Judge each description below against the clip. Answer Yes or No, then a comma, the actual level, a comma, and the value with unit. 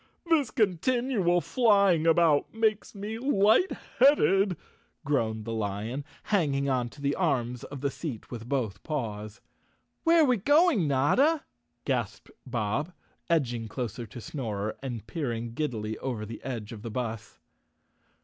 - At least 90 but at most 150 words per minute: Yes, average, 140 wpm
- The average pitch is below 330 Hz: Yes, medium, 140 Hz